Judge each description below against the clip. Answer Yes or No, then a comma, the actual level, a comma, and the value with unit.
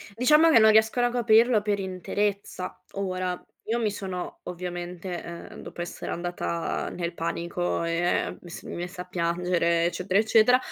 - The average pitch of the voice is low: No, medium, 180 Hz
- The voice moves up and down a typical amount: Yes, average, 3.8 semitones